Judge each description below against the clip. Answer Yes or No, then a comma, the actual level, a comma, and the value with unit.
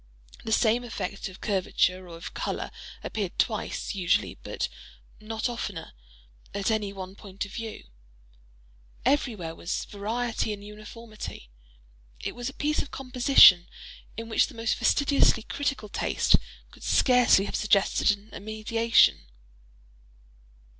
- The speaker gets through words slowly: Yes, slow, 125 wpm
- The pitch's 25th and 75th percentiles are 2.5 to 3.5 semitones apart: Yes, average, 3.0 semitones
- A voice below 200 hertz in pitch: No, high, 215 Hz